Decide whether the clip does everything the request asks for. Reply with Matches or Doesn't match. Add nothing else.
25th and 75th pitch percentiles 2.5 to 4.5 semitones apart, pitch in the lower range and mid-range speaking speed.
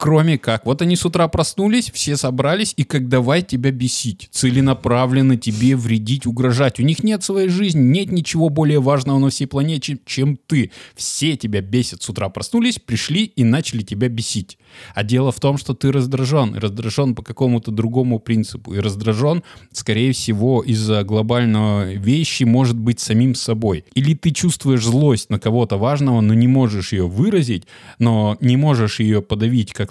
Doesn't match